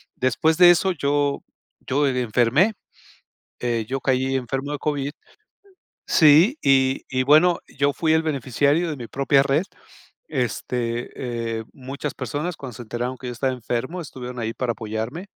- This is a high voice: No, low, 135 Hz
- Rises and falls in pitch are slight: No, average, 3.3 semitones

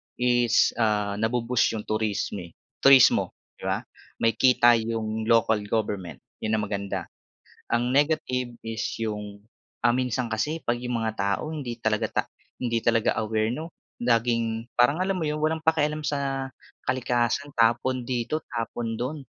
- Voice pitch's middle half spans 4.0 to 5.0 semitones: No, average, 2.7 semitones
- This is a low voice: Yes, low, 120 Hz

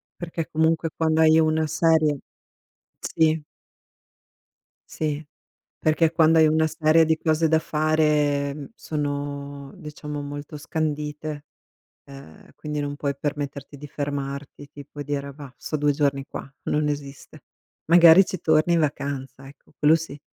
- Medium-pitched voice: Yes, medium, 150 Hz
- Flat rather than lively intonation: Yes, narrow, 1.8 semitones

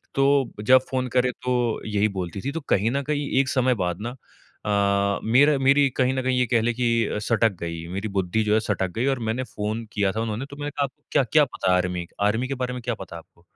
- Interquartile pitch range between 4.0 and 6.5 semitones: Yes, average, 4.4 semitones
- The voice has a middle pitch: No, low, 115 Hz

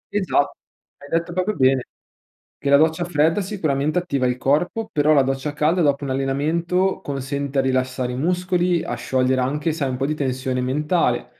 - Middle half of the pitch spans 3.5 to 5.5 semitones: Yes, average, 4.2 semitones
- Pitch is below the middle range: No, medium, 145 Hz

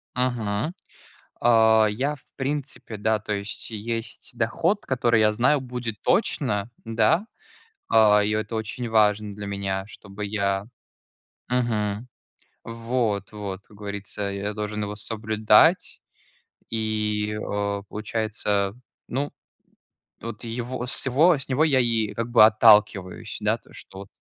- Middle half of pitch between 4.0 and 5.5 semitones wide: No, narrow, 2.6 semitones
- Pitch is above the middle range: No, low, 110 Hz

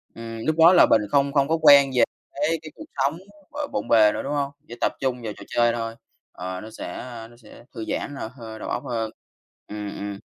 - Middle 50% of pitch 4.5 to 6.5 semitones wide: No, average, 4.1 semitones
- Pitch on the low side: Yes, low, 120 Hz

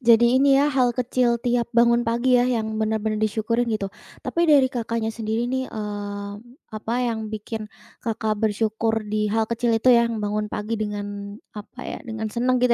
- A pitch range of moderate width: No, narrow, 2.0 semitones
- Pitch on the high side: Yes, high, 225 Hz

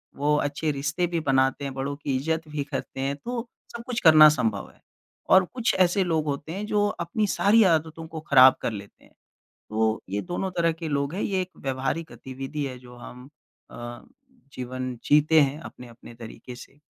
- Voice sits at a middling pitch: Yes, medium, 145 Hz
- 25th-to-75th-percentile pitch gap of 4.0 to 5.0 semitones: Yes, average, 4.3 semitones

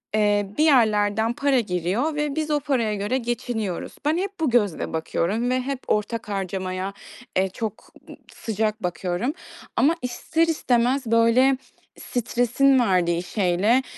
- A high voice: Yes, high, 230 Hz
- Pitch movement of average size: Yes, average, 4.8 semitones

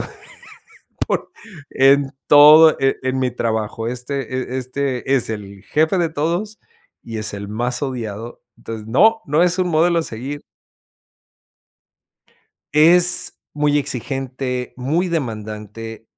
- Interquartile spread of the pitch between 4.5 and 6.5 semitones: Yes, average, 5.1 semitones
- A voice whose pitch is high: No, low, 130 Hz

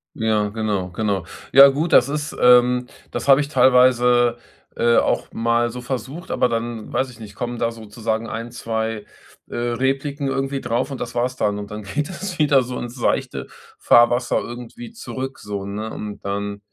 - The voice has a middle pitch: No, low, 120 Hz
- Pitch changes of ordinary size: Yes, average, 3.0 semitones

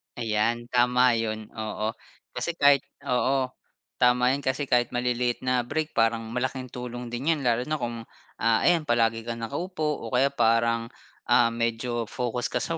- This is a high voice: No, low, 120 Hz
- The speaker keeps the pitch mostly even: Yes, narrow, 2.1 semitones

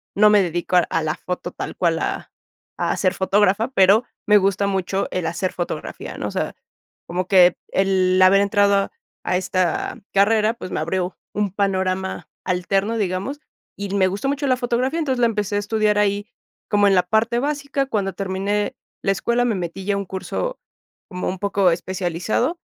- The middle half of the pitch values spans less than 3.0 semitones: Yes, narrow, 2.5 semitones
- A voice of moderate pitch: No, high, 195 Hz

